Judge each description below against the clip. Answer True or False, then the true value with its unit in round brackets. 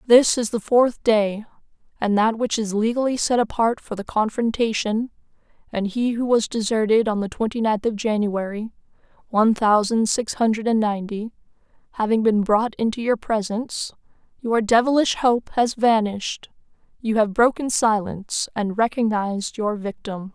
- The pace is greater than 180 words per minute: False (150 wpm)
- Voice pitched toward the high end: True (220 Hz)